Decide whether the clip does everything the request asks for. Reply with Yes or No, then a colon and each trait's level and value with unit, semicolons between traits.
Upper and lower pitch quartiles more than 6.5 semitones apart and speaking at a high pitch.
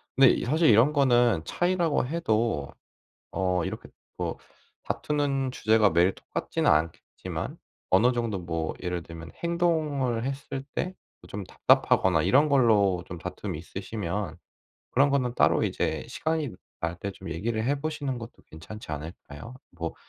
No: wide, 7.7 semitones; low, 115 Hz